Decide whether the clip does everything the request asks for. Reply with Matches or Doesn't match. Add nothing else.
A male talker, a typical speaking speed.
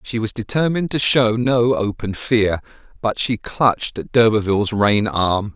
Matches